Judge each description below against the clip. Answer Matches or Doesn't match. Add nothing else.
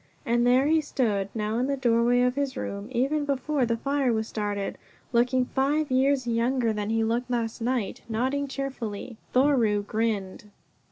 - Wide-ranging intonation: Doesn't match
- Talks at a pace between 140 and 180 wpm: Matches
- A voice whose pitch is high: Matches